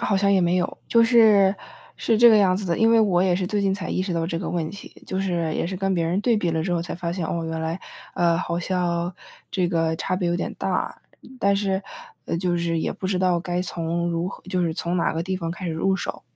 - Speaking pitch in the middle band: Yes, medium, 180 Hz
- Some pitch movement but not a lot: No, narrow, 2.3 semitones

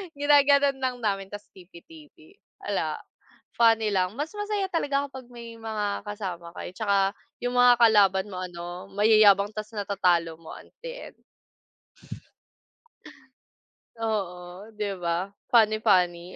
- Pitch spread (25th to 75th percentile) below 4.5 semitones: No, average, 4.9 semitones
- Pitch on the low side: No, high, 210 Hz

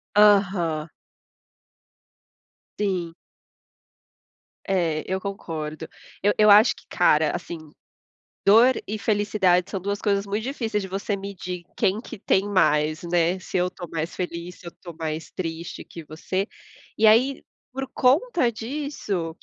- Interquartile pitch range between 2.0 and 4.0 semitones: Yes, average, 3.7 semitones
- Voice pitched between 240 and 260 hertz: No, high, 190 Hz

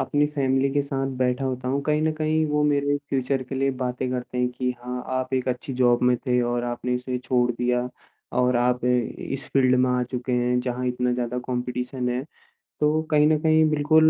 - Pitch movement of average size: No, narrow, 2.0 semitones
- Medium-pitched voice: No, low, 125 Hz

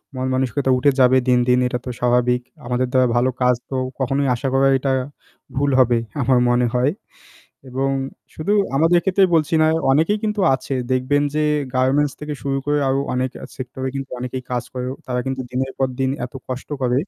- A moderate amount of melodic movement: No, narrow, 1.9 semitones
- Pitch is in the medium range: No, low, 130 Hz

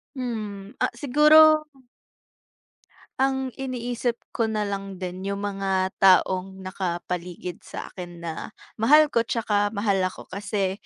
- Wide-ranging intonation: No, average, 4.3 semitones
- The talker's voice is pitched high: Yes, high, 200 Hz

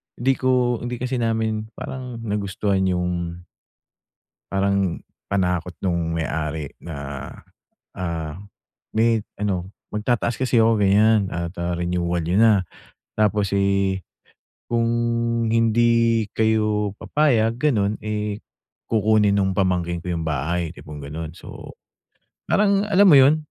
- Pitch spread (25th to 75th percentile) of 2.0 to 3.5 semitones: No, average, 4.6 semitones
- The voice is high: No, low, 100 Hz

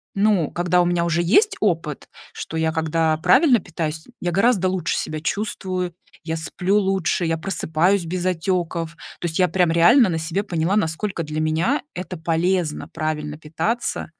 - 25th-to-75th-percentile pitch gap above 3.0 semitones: No, average, 2.7 semitones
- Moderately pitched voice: Yes, medium, 175 Hz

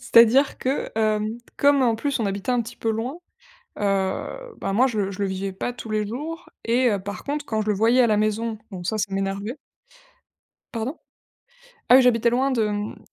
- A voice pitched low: No, high, 225 Hz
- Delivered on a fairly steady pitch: No, average, 3.6 semitones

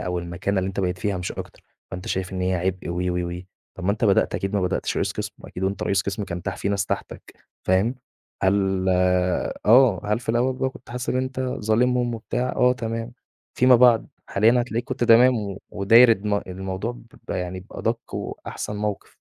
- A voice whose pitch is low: Yes, low, 105 Hz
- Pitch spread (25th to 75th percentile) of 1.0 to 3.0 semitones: No, average, 4.2 semitones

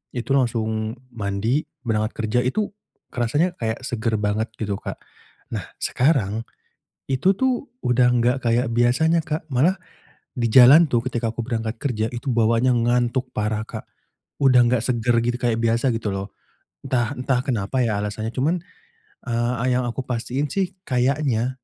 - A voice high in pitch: No, low, 120 Hz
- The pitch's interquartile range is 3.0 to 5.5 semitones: No, narrow, 2.6 semitones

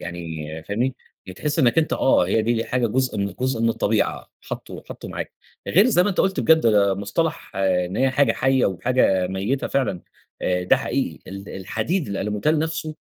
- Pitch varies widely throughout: Yes, wide, 6.5 semitones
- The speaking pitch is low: Yes, low, 115 Hz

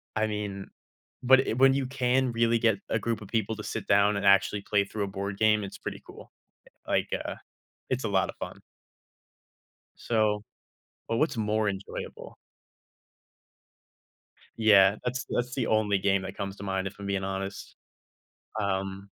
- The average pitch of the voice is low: Yes, low, 105 Hz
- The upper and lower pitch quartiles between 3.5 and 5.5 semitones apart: No, narrow, 2.6 semitones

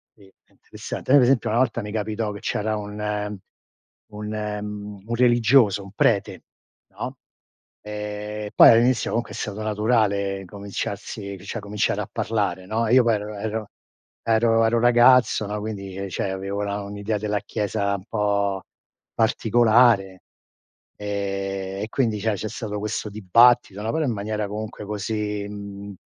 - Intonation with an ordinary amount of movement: No, narrow, 1.8 semitones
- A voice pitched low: Yes, low, 105 Hz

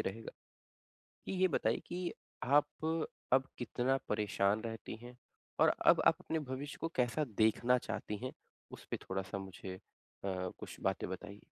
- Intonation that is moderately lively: No, wide, 5.9 semitones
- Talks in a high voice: No, low, 120 Hz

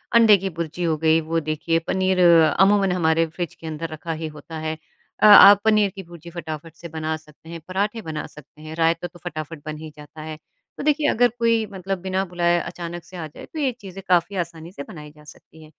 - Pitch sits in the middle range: Yes, medium, 170 Hz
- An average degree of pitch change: Yes, average, 3.3 semitones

